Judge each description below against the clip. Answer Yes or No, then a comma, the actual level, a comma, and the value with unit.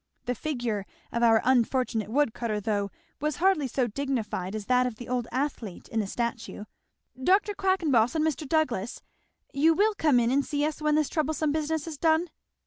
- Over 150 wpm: Yes, average, 185 wpm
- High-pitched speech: Yes, very high, 265 Hz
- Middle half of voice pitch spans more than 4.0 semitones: Yes, average, 5.0 semitones